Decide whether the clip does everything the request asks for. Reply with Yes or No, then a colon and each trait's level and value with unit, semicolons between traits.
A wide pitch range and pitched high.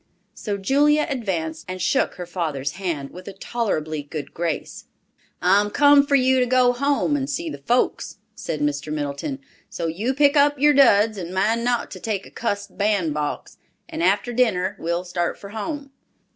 Yes: wide, 7.3 semitones; high, 205 Hz